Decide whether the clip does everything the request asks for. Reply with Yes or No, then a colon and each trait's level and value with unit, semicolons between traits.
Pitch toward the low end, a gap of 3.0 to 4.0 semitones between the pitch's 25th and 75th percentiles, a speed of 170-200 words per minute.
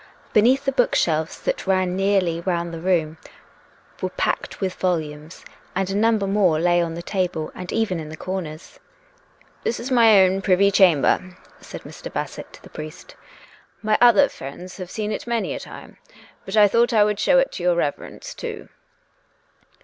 No: medium, 185 Hz; average, 3.7 semitones; average, 185 wpm